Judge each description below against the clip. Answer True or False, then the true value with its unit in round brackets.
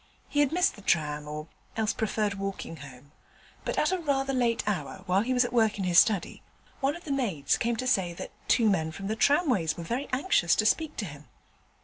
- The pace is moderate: False (225 wpm)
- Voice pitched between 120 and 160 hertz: False (215 Hz)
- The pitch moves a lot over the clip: True (7.1 semitones)